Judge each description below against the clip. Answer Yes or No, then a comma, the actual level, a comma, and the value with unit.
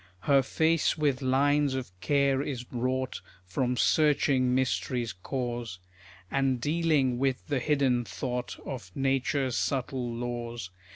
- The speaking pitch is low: Yes, low, 130 Hz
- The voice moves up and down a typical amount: No, narrow, 2.3 semitones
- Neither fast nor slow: No, slow, 120 wpm